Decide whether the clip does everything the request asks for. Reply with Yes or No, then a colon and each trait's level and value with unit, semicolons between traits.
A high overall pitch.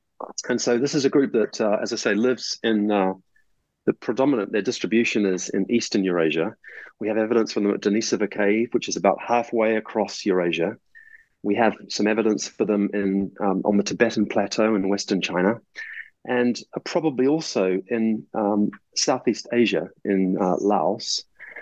No: low, 110 Hz